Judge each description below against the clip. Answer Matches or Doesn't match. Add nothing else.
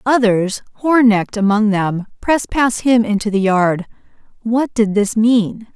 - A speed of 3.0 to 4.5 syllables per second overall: Matches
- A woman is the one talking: Matches